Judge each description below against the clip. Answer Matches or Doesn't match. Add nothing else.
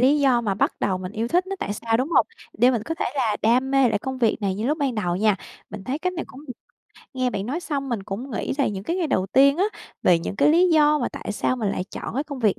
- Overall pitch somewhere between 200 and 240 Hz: Doesn't match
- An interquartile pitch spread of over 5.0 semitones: Matches